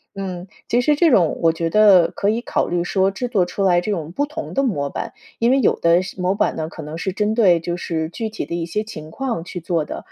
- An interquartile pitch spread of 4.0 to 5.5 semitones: Yes, average, 4.5 semitones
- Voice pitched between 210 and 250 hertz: No, medium, 185 Hz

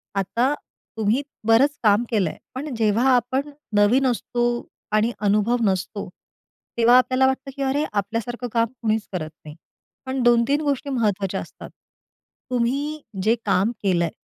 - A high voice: Yes, high, 235 Hz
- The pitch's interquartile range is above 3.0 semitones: Yes, average, 4.0 semitones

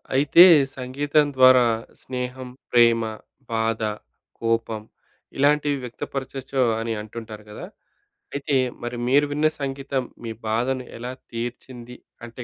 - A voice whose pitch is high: No, low, 125 Hz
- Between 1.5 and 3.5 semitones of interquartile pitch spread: Yes, average, 2.9 semitones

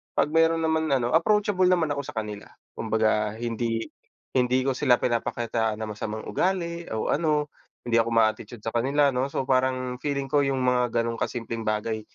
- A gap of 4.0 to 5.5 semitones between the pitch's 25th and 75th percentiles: Yes, average, 4.4 semitones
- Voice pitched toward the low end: Yes, low, 125 Hz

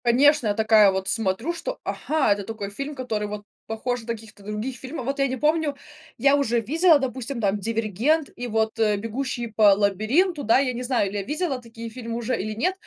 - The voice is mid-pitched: No, high, 235 Hz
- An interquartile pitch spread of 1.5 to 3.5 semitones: No, average, 4.4 semitones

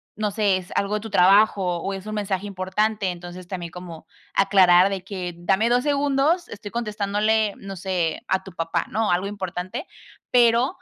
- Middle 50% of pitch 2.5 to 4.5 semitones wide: Yes, average, 2.9 semitones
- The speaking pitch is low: No, high, 195 Hz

